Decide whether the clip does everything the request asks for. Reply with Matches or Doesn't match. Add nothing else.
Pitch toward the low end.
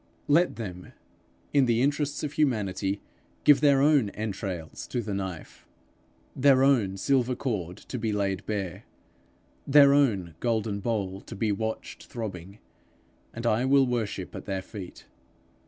Matches